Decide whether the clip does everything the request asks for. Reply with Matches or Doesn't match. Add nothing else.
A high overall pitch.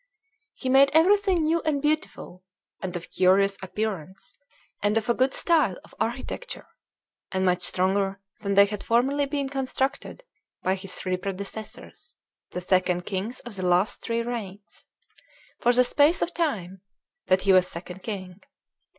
Matches